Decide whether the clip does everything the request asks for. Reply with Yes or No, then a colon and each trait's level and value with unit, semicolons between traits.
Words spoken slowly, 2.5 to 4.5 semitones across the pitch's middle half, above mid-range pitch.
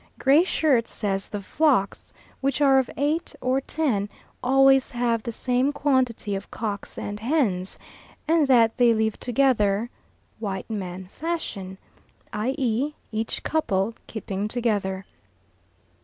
No: slow, 125 wpm; average, 4.9 semitones; high, 235 Hz